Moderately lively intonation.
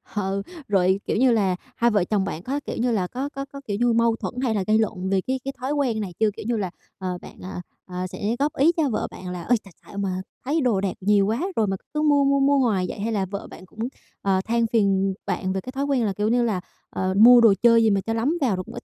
Yes: average, 4.4 semitones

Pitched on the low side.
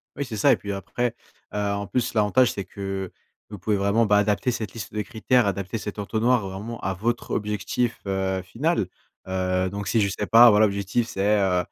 Yes: low, 105 Hz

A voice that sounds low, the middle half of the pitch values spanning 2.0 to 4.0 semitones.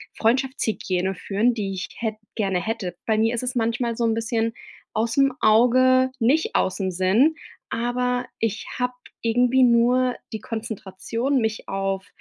No: high, 230 Hz; average, 2.8 semitones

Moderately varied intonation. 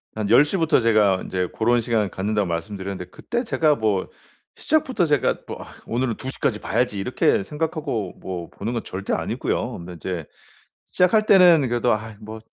No: wide, 7.1 semitones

